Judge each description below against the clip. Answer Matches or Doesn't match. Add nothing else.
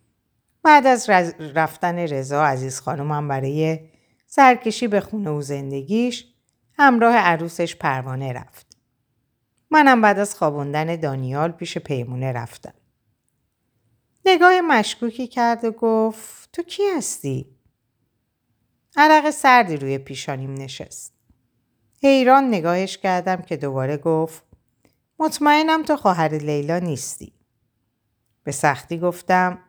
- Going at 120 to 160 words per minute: Doesn't match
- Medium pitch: Matches